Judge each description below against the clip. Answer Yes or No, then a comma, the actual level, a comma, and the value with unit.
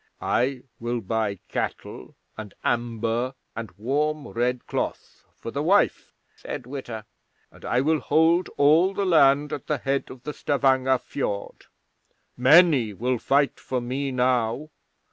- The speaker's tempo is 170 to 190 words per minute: No, slow, 135 wpm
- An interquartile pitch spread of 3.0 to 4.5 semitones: Yes, average, 3.5 semitones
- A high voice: No, low, 130 Hz